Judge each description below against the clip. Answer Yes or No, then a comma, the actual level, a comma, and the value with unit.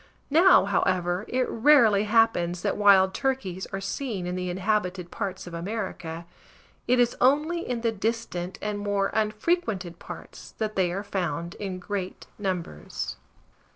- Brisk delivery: No, average, 145 wpm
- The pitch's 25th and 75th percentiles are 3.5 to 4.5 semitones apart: Yes, average, 3.8 semitones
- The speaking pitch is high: Yes, high, 200 Hz